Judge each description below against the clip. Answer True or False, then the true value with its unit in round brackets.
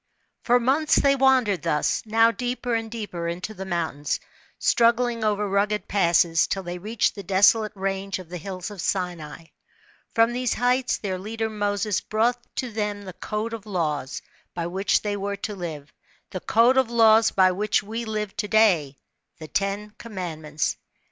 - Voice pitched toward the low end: False (205 Hz)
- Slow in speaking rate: False (170 wpm)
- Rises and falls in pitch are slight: False (3.8 semitones)